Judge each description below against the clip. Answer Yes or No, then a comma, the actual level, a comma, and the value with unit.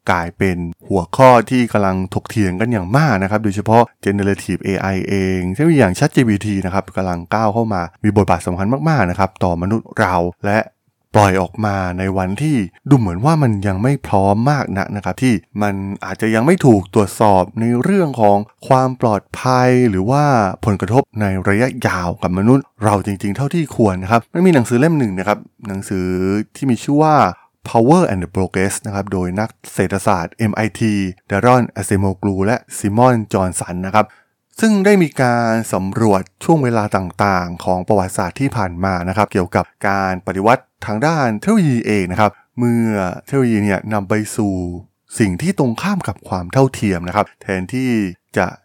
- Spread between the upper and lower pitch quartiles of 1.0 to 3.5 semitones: No, average, 4.3 semitones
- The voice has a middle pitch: No, low, 105 Hz